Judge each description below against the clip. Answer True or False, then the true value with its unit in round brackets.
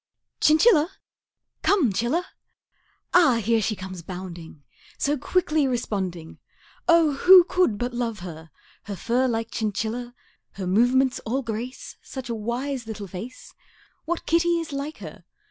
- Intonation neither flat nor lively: False (6.2 semitones)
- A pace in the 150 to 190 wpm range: False (135 wpm)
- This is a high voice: True (240 Hz)